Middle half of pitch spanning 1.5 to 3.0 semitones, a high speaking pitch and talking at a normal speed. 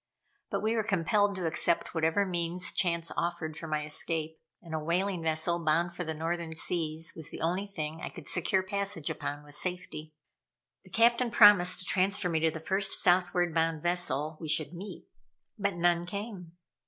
No: average, 2.7 semitones; medium, 170 Hz; average, 180 wpm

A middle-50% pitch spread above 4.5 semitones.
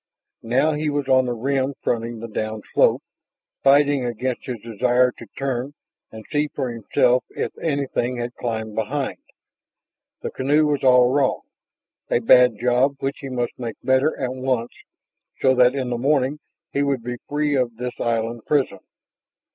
No: narrow, 2.6 semitones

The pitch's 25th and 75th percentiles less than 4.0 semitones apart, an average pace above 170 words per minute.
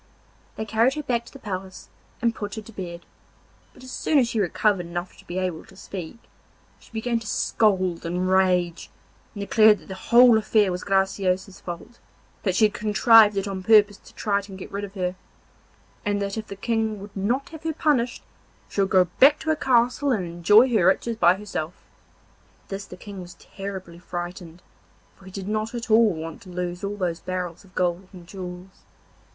Yes: average, 3.3 semitones; average, 200 wpm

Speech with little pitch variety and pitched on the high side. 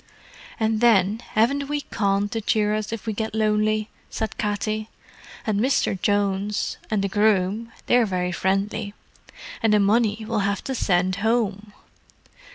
Yes: narrow, 1.8 semitones; high, 210 Hz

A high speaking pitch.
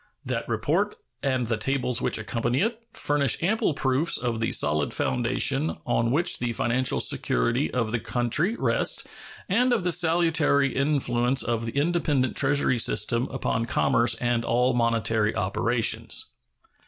No: low, 125 Hz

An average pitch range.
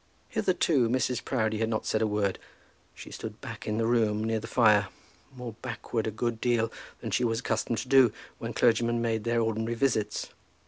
No: narrow, 1.5 semitones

